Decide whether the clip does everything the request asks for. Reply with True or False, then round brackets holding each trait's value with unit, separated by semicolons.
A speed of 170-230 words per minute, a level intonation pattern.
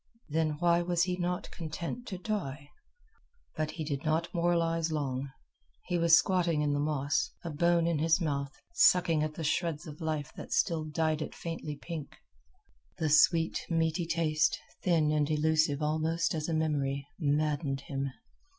False (160 wpm; 2.1 semitones)